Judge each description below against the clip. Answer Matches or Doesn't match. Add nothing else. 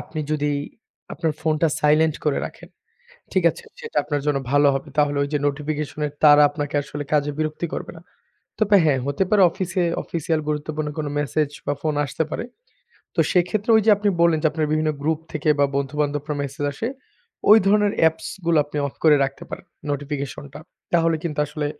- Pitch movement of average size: Doesn't match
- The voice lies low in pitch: Doesn't match